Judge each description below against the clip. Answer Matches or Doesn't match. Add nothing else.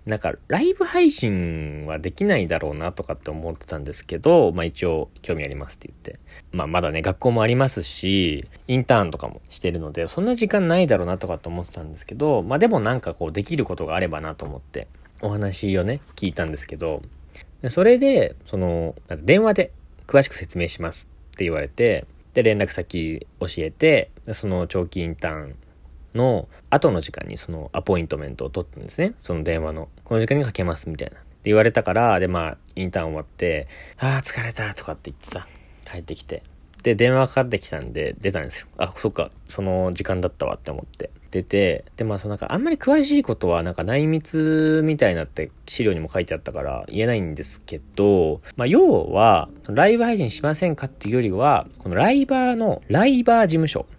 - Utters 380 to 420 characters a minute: Matches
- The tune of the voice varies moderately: Doesn't match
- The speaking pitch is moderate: Doesn't match